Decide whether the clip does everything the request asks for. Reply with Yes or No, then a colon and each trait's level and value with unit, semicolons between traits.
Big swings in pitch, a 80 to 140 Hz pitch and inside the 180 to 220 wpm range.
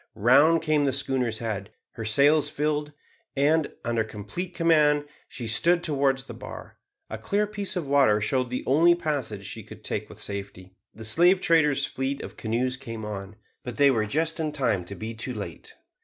Yes: wide, 5.7 semitones; low, 135 Hz; average, 185 wpm